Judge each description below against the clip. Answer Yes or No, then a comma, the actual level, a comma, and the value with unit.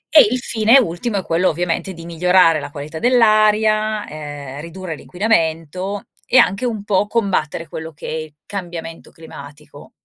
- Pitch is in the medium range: Yes, medium, 175 Hz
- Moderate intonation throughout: Yes, average, 5.0 semitones